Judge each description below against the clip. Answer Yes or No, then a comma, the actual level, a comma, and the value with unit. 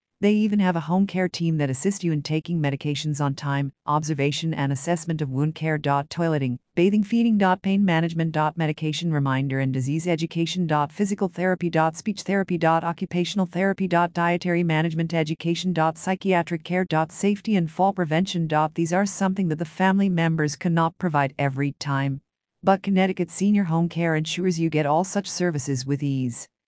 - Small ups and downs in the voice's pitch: No, average, 3.3 semitones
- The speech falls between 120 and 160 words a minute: No, average, 180 wpm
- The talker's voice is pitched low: No, medium, 165 Hz